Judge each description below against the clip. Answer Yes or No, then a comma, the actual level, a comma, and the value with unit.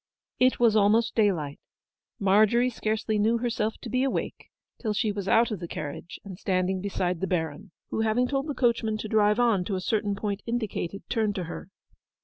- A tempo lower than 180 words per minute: No, average, 190 wpm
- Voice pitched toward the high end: Yes, high, 210 Hz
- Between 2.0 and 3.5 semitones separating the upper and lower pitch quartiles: Yes, average, 3.1 semitones